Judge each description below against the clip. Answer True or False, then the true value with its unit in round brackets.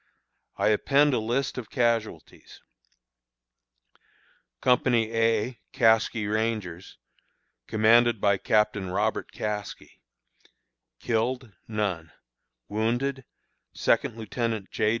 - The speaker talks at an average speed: False (85 wpm)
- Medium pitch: False (110 Hz)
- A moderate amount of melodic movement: False (2.1 semitones)